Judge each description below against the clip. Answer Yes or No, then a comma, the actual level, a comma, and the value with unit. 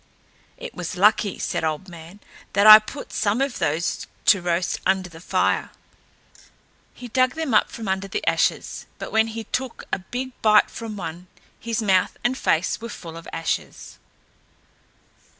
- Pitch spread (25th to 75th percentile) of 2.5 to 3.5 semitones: No, average, 4.3 semitones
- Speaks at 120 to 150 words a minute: No, average, 165 wpm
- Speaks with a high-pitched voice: Yes, high, 200 Hz